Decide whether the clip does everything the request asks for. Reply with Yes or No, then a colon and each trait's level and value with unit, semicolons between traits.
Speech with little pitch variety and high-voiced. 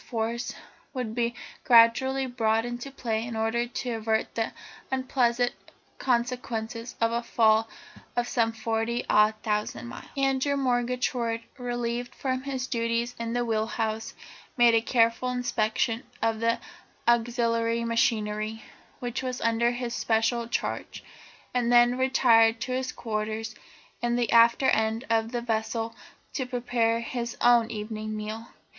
Yes: narrow, 1.5 semitones; high, 235 Hz